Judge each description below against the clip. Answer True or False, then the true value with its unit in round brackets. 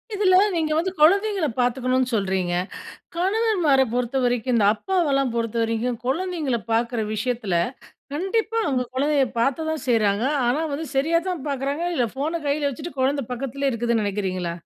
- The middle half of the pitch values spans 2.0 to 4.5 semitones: False (5.4 semitones)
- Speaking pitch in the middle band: False (265 Hz)